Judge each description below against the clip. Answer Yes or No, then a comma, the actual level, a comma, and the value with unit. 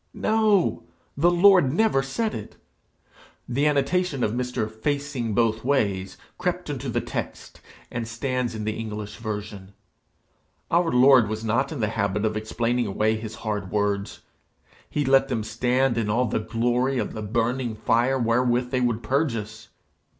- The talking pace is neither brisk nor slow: Yes, average, 150 wpm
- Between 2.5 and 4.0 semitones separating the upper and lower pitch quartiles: Yes, average, 3.7 semitones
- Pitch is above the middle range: No, low, 120 Hz